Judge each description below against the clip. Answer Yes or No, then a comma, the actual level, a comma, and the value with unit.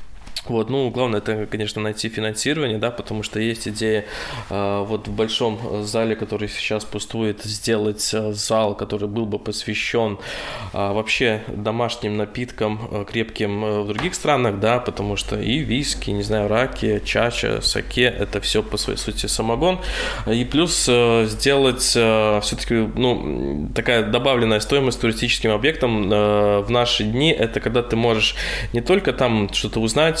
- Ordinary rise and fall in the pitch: No, narrow, 2.3 semitones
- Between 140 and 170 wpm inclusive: Yes, average, 155 wpm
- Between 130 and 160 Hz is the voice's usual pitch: No, low, 110 Hz